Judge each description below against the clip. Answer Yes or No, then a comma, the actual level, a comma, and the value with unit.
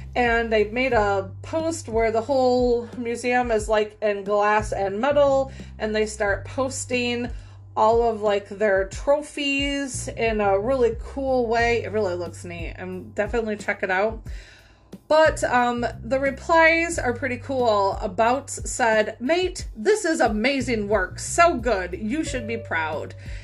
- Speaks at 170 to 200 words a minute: No, average, 150 wpm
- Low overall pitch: No, high, 230 Hz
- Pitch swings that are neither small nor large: Yes, average, 4.5 semitones